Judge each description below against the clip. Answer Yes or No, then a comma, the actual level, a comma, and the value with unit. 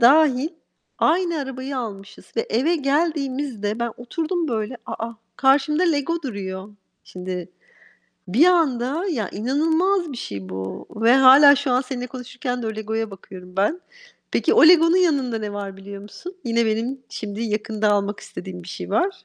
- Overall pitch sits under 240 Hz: No, very high, 250 Hz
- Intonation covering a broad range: Yes, wide, 6.2 semitones